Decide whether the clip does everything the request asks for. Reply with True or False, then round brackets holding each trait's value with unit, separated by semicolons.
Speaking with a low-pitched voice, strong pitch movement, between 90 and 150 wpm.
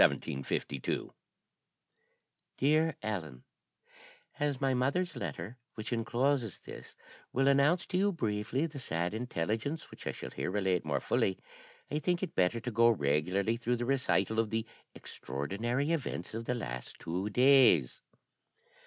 True (115 Hz; 6.5 semitones; 140 wpm)